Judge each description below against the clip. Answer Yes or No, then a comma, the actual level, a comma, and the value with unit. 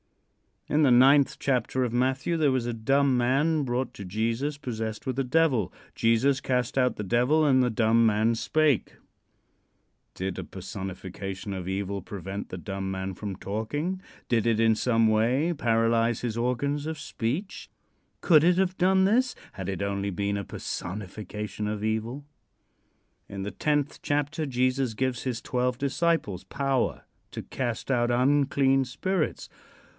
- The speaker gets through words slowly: No, average, 155 wpm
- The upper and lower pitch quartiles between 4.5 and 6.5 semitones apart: Yes, average, 4.8 semitones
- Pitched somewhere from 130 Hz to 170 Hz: No, low, 120 Hz